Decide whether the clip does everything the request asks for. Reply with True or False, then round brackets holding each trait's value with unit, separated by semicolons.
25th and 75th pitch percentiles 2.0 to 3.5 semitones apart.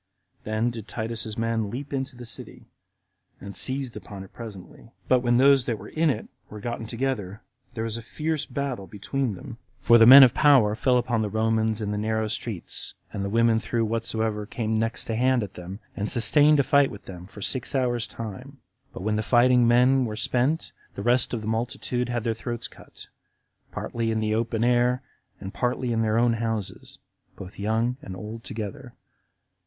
True (2.4 semitones)